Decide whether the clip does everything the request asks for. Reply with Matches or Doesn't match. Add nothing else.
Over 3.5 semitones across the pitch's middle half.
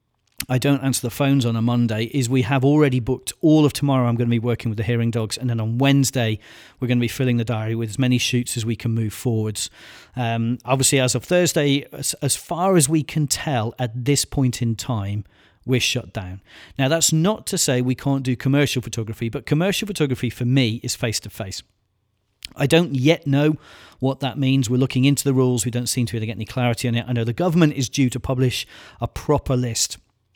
Doesn't match